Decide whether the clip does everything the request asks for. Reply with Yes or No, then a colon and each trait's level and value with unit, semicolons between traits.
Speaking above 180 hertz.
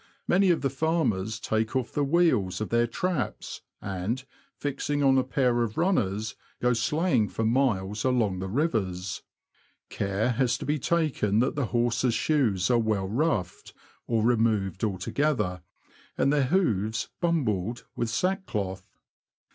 No: low, 120 Hz